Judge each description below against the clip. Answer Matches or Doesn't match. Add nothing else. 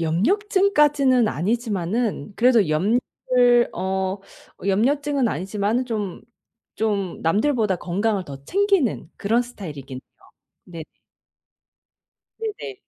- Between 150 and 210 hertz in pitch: Doesn't match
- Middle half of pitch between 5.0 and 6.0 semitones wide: Matches